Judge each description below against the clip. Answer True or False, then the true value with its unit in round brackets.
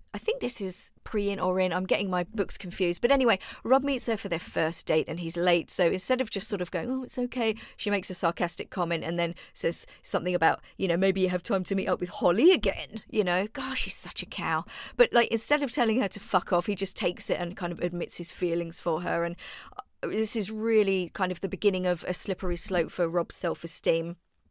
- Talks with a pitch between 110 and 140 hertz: False (185 Hz)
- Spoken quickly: True (245 wpm)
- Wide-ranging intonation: False (4.0 semitones)